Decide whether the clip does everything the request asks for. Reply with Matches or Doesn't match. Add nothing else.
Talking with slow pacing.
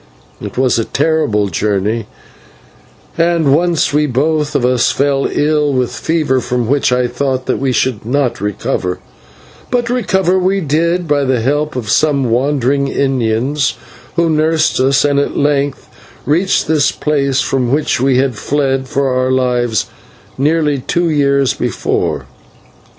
Doesn't match